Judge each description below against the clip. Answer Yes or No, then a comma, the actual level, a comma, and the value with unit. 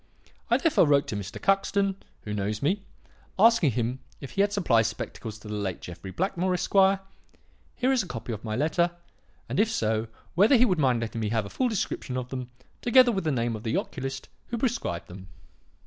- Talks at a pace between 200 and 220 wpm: Yes, fast, 205 wpm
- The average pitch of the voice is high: No, low, 135 Hz